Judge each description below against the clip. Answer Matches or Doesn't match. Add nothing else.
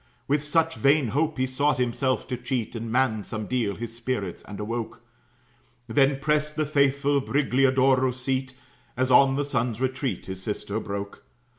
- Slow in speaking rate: Doesn't match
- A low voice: Matches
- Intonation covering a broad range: Doesn't match